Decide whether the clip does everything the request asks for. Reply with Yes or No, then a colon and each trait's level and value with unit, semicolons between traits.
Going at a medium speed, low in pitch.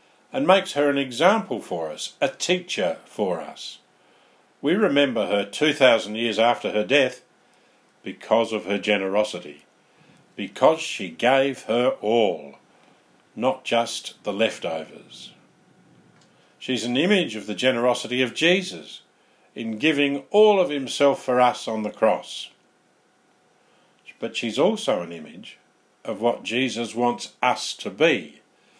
No: slow, 130 wpm; low, 125 Hz